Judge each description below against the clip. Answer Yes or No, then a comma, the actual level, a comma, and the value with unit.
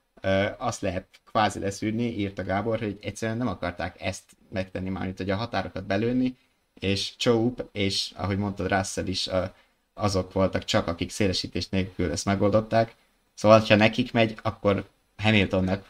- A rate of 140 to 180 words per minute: Yes, average, 150 wpm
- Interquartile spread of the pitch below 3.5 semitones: Yes, narrow, 2.6 semitones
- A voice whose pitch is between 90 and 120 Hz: Yes, low, 100 Hz